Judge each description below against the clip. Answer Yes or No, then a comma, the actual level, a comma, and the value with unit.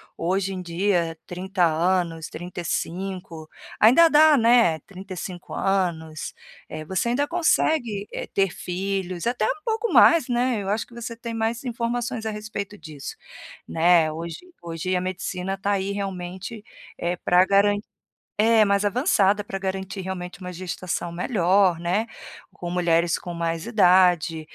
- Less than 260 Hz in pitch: Yes, high, 190 Hz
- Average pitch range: Yes, average, 3.7 semitones